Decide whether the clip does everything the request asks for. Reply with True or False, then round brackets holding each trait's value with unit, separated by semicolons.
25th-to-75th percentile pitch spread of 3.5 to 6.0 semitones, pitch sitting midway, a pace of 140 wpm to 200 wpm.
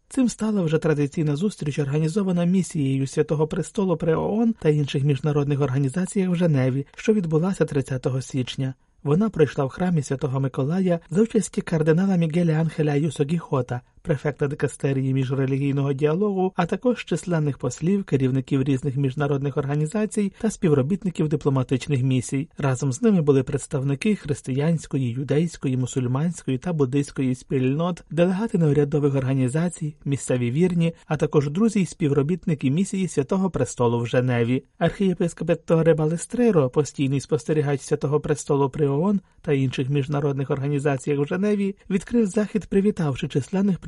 False (4.3 semitones; 150 Hz; 130 wpm)